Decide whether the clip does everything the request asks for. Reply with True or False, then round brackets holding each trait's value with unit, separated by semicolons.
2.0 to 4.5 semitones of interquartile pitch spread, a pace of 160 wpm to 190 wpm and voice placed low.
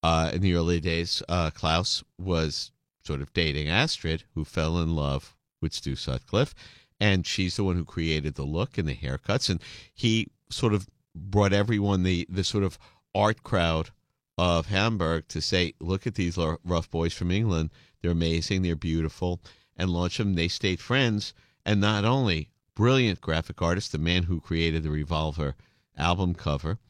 True (3.7 semitones; 175 wpm; 90 Hz)